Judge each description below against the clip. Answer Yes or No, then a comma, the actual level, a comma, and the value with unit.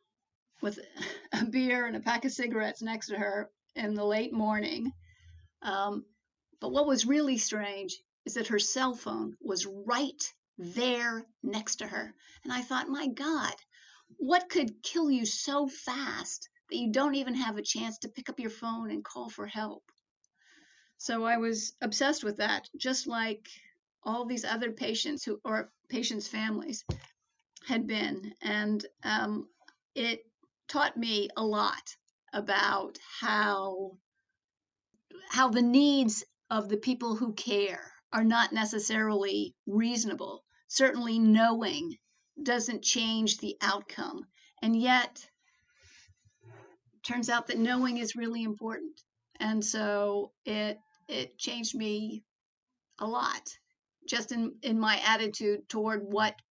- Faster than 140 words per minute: No, slow, 135 wpm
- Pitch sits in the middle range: No, high, 230 Hz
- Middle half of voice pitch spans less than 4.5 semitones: Yes, average, 3.3 semitones